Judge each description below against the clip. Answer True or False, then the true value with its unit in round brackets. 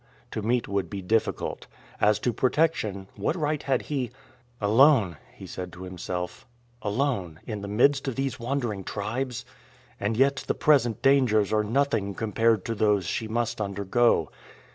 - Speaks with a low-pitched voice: True (110 Hz)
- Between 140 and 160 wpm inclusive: True (155 wpm)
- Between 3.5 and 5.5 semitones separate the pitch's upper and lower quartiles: True (4.8 semitones)